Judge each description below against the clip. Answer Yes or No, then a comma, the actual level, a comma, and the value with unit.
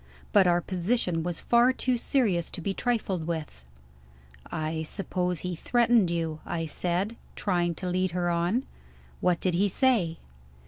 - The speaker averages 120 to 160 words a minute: Yes, average, 150 wpm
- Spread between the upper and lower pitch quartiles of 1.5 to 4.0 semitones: Yes, average, 3.3 semitones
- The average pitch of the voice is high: No, medium, 180 Hz